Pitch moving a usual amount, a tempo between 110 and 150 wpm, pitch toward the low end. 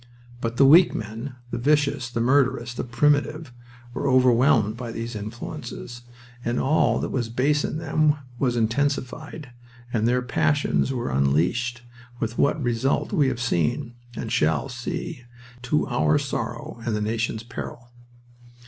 Yes: average, 3.5 semitones; average, 145 wpm; low, 120 Hz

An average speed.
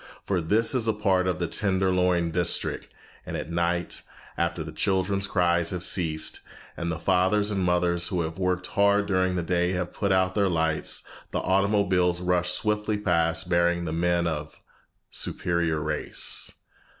Yes: average, 165 wpm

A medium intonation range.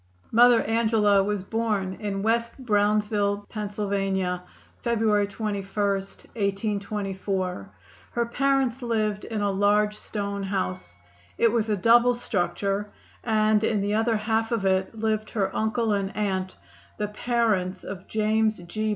No: narrow, 2.2 semitones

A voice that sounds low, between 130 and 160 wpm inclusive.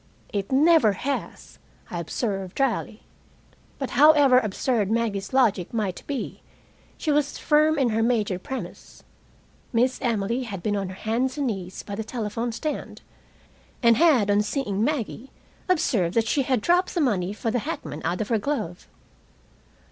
No: high, 230 Hz; average, 155 wpm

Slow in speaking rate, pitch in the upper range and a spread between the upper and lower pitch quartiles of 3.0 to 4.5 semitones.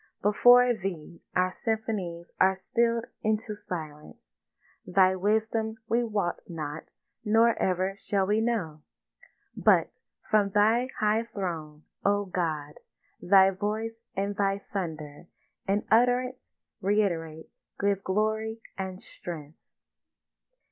Yes: slow, 105 wpm; high, 200 Hz; average, 3.8 semitones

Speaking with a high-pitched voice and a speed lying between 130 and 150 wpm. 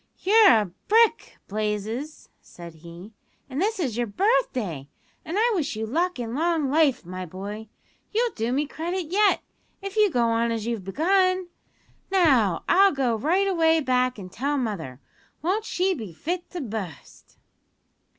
No: very high, 275 Hz; average, 160 wpm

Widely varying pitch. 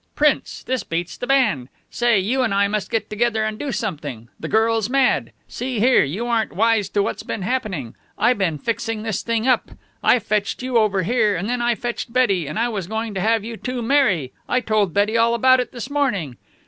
No: average, 3.4 semitones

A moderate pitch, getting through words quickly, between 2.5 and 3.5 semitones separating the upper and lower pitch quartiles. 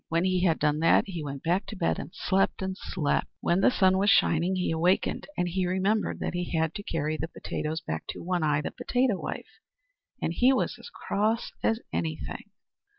Yes: medium, 180 Hz; fast, 210 wpm; average, 3.1 semitones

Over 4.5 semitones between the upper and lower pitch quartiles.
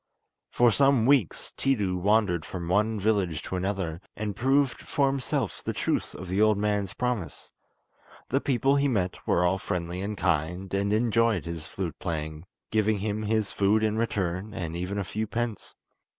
No: average, 3.7 semitones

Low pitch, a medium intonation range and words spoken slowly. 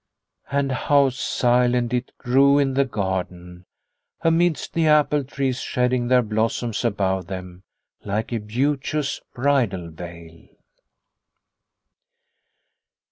No: low, 125 Hz; wide, 6.2 semitones; slow, 100 wpm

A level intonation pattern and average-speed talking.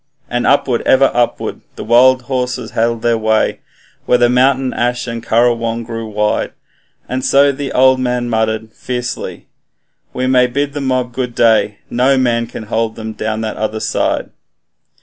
Yes: narrow, 2.2 semitones; average, 155 wpm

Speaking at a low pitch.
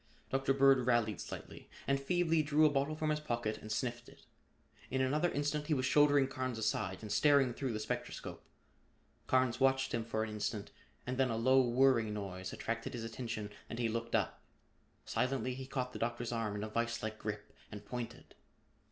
Yes: low, 125 Hz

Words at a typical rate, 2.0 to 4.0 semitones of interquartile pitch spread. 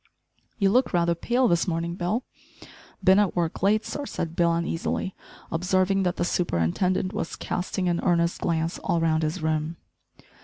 Yes: average, 160 wpm; narrow, 2.4 semitones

